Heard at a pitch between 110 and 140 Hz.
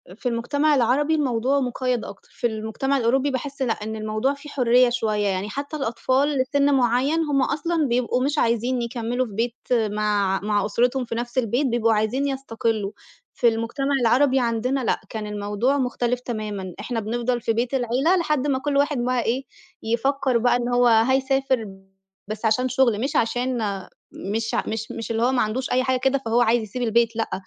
No: high, 245 Hz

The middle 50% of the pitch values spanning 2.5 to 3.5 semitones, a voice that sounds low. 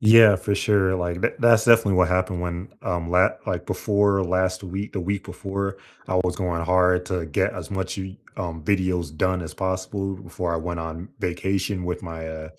No: narrow, 1.9 semitones; very low, 95 Hz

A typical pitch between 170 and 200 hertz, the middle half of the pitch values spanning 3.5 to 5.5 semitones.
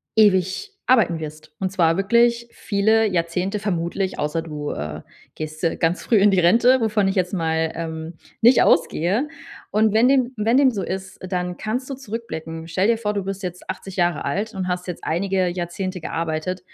Yes: medium, 185 Hz; average, 4.5 semitones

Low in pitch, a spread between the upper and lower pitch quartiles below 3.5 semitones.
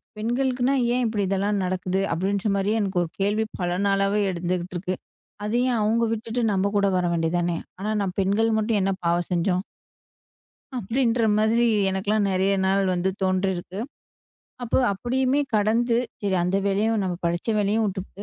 No: high, 200 Hz; average, 3.1 semitones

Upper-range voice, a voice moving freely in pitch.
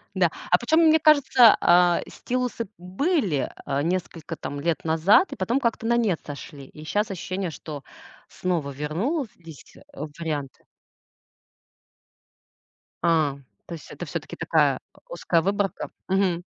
No: medium, 180 Hz; wide, 6.4 semitones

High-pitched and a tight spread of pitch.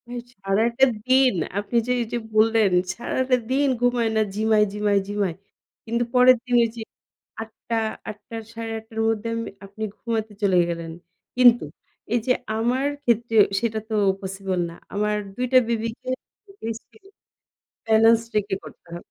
Yes: high, 225 Hz; narrow, 2.2 semitones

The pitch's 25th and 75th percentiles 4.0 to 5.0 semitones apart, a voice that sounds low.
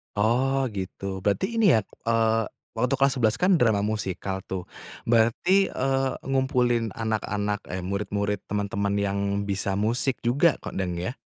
Yes: average, 4.4 semitones; low, 110 Hz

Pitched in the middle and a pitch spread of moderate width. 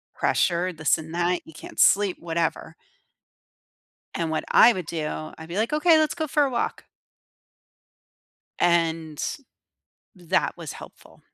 Yes: medium, 170 Hz; average, 4.8 semitones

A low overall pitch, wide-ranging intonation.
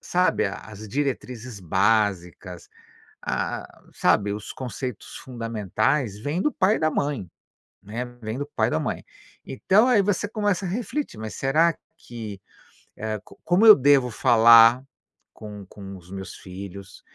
Yes: low, 115 Hz; wide, 6.6 semitones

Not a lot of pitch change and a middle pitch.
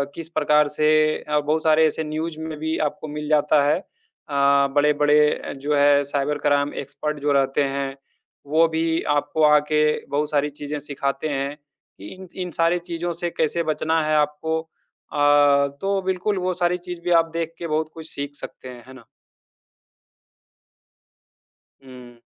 Yes: narrow, 2.0 semitones; medium, 150 Hz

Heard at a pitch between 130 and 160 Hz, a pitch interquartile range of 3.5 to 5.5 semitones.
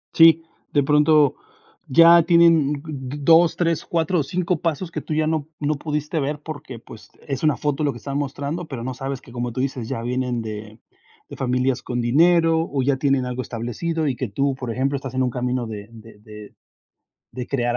Yes: medium, 140 Hz; average, 4.1 semitones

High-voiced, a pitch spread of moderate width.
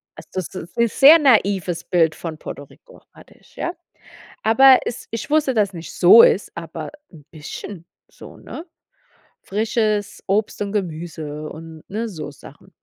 No: high, 195 Hz; wide, 5.8 semitones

